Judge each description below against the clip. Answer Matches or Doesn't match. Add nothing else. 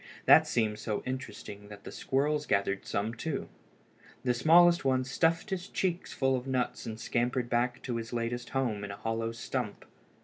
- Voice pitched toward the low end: Matches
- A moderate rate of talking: Matches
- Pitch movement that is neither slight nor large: Matches